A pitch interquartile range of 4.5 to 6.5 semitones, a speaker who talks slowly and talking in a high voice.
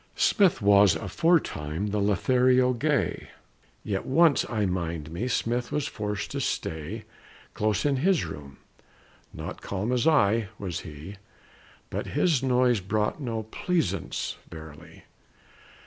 No: wide, 5.4 semitones; slow, 125 wpm; low, 110 Hz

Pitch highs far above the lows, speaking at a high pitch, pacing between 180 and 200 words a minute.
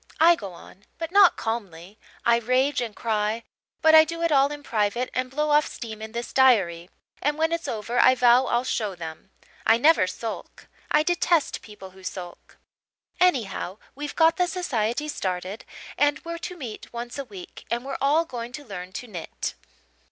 Yes: wide, 6.1 semitones; high, 240 Hz; average, 185 wpm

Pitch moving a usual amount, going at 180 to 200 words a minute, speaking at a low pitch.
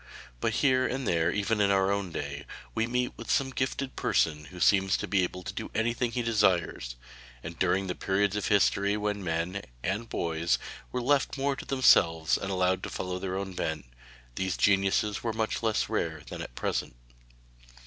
Yes: average, 4.0 semitones; average, 190 wpm; low, 100 Hz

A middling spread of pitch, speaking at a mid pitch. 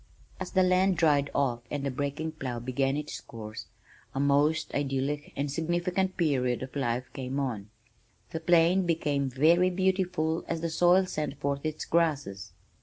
Yes: average, 3.9 semitones; medium, 145 Hz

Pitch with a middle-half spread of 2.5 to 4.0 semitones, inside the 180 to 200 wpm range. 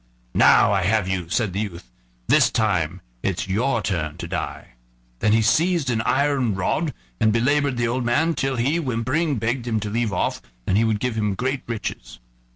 No: average, 4.9 semitones; average, 190 wpm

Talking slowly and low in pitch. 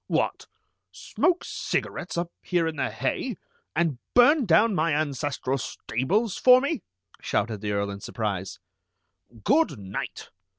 No: slow, 130 wpm; medium, 155 Hz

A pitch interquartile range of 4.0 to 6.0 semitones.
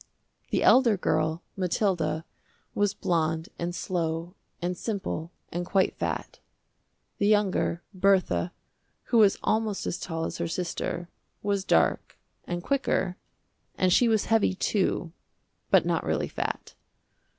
No: average, 3.2 semitones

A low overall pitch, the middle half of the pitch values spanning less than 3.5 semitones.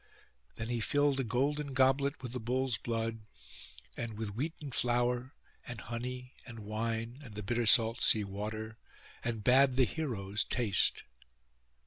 Yes: low, 120 Hz; average, 2.7 semitones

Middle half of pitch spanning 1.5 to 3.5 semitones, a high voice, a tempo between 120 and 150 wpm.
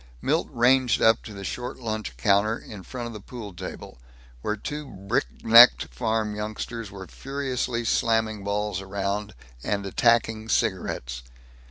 No: average, 2.9 semitones; low, 110 Hz; average, 140 wpm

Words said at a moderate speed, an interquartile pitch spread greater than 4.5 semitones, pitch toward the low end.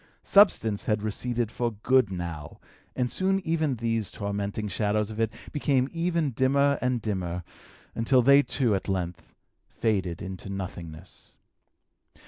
No: slow, 130 wpm; average, 5.1 semitones; low, 110 Hz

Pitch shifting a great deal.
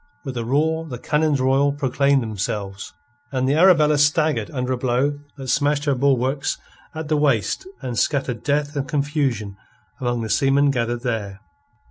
No: average, 3.2 semitones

